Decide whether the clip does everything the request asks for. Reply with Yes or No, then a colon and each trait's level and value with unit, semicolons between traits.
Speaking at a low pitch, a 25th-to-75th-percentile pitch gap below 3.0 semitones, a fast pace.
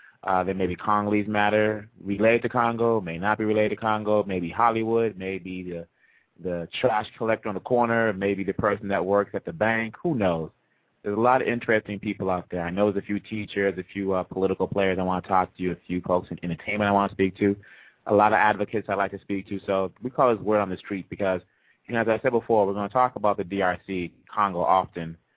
Yes: low, 100 Hz; narrow, 2.5 semitones; fast, 245 wpm